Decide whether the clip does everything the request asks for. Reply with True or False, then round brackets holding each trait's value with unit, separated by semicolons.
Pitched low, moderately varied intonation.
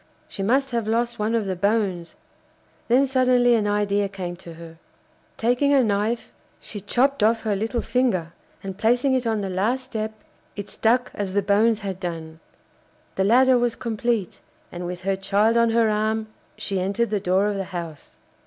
False (215 Hz; 3.5 semitones)